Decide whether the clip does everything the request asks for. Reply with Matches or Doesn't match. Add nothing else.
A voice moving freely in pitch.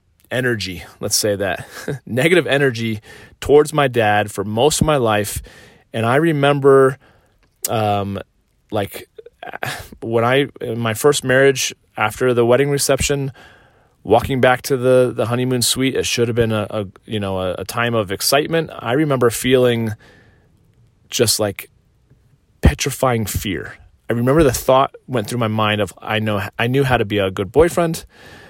Doesn't match